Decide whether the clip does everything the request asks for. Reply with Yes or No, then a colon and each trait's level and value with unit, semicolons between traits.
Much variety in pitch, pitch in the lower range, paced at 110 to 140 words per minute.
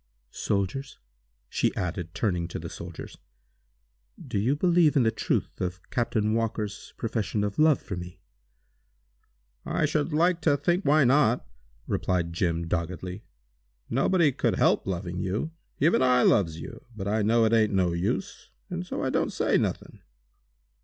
No: wide, 7.6 semitones; low, 110 Hz; average, 155 wpm